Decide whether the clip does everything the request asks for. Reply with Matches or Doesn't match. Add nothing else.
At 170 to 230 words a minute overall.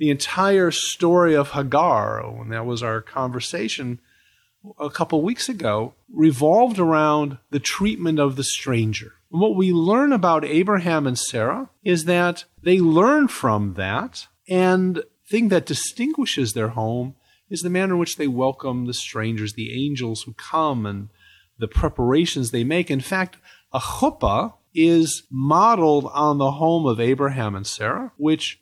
Doesn't match